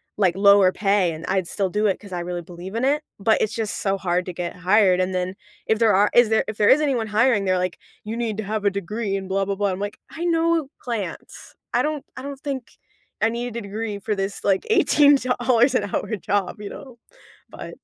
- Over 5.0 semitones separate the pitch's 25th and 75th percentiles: No, average, 3.7 semitones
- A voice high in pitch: Yes, high, 205 Hz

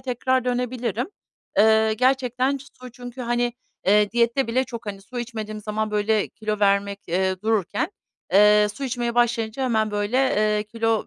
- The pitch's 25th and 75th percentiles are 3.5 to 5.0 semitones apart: No, average, 2.9 semitones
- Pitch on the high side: Yes, high, 225 Hz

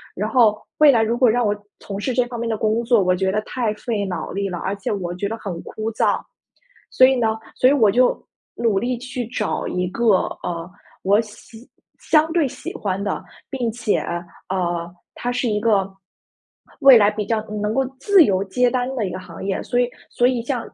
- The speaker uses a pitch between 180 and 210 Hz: No, high, 220 Hz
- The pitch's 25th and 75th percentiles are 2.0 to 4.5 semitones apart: Yes, average, 3.8 semitones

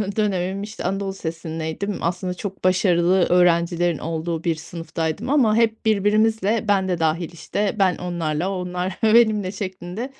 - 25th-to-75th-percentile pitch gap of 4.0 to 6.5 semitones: No, average, 3.3 semitones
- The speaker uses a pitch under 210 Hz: Yes, medium, 185 Hz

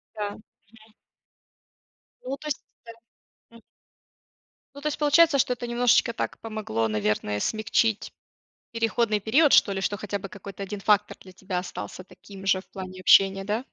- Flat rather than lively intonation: No, average, 3.4 semitones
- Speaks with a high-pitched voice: Yes, high, 210 Hz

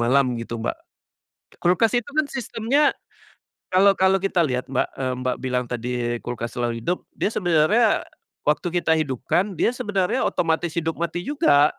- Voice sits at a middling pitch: Yes, medium, 165 Hz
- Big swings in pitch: Yes, wide, 7.5 semitones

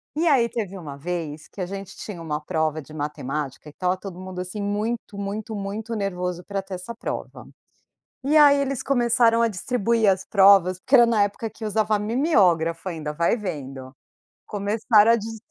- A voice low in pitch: No, high, 200 Hz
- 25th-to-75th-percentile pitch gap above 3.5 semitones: Yes, average, 4.4 semitones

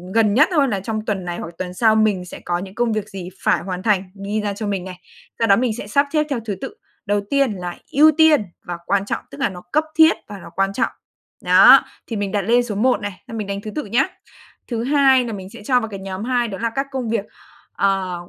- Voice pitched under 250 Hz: Yes, high, 215 Hz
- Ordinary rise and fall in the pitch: Yes, average, 4.0 semitones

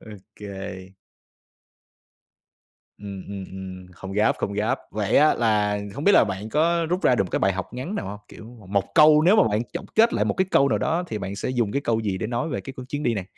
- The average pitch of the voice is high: No, low, 110 Hz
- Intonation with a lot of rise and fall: Yes, wide, 6.3 semitones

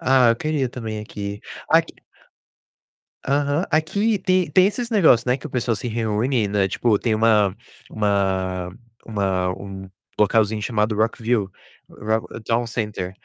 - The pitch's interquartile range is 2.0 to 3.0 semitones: No, average, 4.2 semitones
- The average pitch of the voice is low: Yes, low, 110 Hz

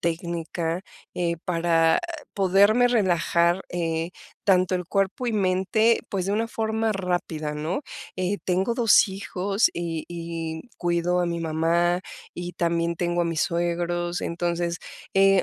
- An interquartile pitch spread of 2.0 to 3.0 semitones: Yes, narrow, 2.4 semitones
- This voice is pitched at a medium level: Yes, medium, 175 Hz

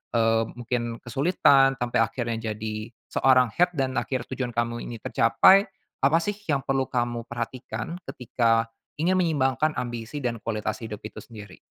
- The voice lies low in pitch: Yes, low, 120 Hz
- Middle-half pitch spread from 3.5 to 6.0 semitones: No, average, 2.8 semitones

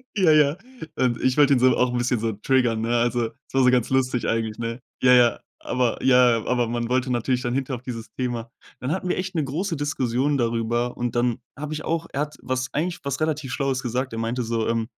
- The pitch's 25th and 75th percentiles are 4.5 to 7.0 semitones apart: No, average, 2.7 semitones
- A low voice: Yes, low, 125 Hz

